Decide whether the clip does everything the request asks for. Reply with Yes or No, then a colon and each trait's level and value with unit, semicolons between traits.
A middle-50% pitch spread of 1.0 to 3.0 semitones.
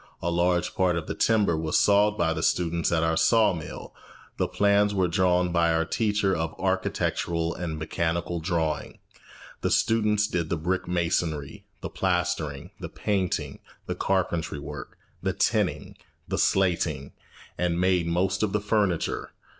Yes: average, 2.7 semitones